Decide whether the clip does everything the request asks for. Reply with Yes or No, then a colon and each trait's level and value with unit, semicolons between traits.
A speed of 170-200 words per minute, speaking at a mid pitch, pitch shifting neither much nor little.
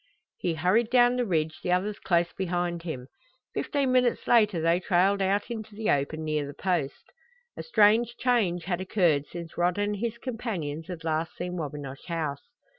Yes: average, 175 wpm; medium, 180 Hz; average, 4.8 semitones